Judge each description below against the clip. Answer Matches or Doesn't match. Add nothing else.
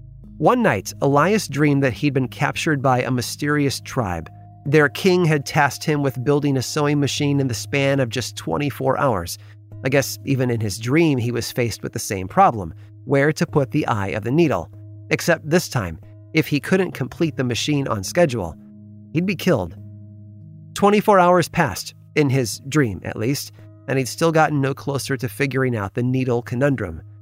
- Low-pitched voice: Matches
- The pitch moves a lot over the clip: Matches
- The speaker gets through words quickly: Doesn't match